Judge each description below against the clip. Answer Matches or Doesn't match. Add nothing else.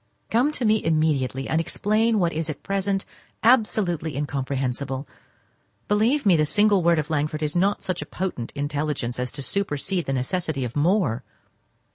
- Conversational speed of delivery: Matches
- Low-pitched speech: Doesn't match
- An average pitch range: Doesn't match